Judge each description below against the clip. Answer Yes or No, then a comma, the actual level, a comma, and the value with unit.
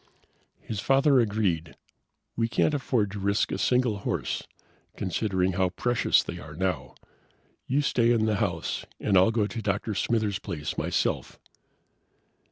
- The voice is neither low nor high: No, low, 105 Hz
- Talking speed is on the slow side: No, average, 145 wpm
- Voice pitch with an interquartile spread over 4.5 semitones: No, average, 3.8 semitones